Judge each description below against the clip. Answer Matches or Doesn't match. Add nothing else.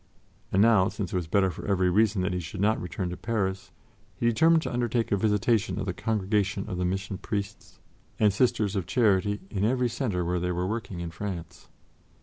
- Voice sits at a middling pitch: Doesn't match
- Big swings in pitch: Doesn't match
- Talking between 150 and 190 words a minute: Doesn't match